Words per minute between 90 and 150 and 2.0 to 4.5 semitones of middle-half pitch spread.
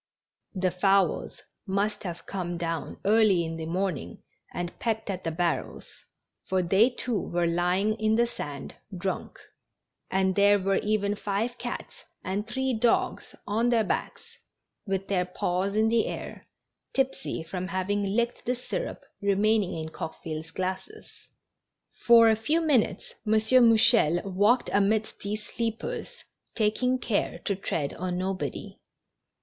Yes: average, 140 wpm; average, 3.5 semitones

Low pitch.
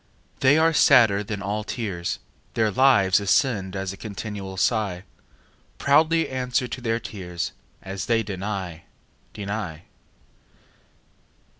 Yes: low, 105 Hz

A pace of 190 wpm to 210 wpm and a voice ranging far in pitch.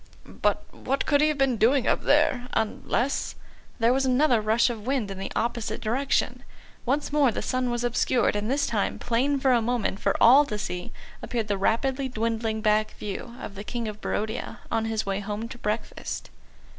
No: average, 195 wpm; average, 3.4 semitones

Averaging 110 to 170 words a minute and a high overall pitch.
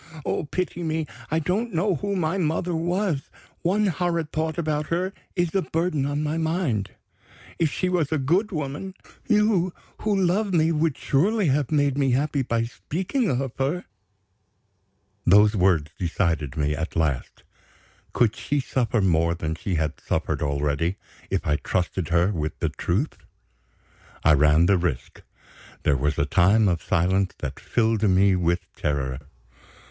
No: average, 155 wpm; low, 135 Hz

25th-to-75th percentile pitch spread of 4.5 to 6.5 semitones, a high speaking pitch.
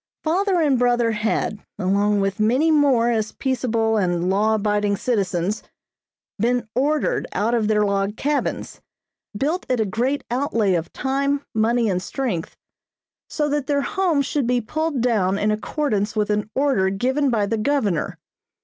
Yes: average, 5.1 semitones; high, 230 Hz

